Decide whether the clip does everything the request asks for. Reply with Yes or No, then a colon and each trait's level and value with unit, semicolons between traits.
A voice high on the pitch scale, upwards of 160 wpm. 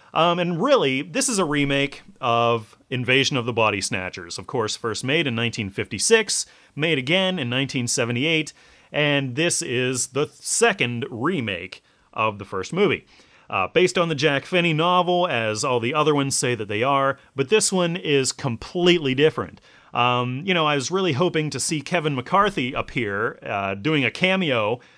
No: medium, 140 Hz; average, 170 wpm